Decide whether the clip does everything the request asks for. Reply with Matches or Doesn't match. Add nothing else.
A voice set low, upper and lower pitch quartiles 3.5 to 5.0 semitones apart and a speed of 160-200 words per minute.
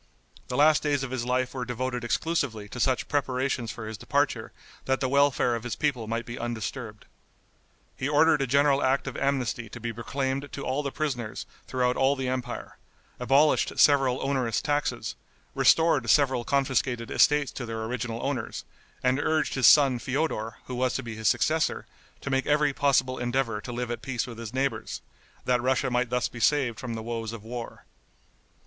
Doesn't match